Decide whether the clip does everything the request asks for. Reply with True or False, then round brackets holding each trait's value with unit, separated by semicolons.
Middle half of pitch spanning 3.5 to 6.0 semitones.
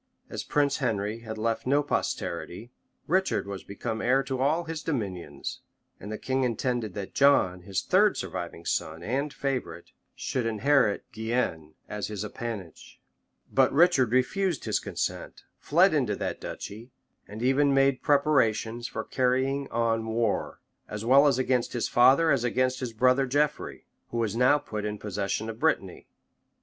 True (4.2 semitones)